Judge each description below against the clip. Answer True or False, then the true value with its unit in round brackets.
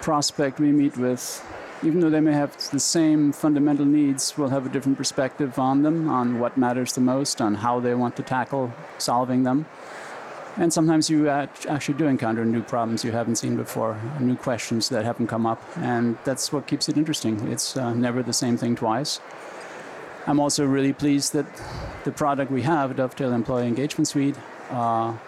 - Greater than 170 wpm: True (185 wpm)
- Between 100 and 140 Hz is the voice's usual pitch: True (135 Hz)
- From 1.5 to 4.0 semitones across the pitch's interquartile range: True (3.2 semitones)